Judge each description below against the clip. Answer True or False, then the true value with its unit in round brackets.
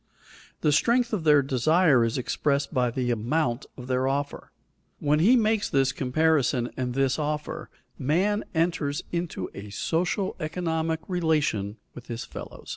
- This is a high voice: False (150 Hz)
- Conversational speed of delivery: True (145 wpm)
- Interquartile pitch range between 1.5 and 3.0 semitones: False (4.4 semitones)